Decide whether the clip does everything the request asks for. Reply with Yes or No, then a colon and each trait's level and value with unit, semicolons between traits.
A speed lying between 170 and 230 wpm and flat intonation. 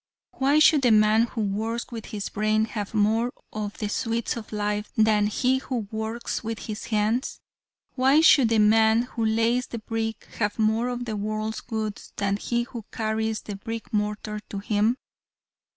Yes: average, 175 wpm; narrow, 1.7 semitones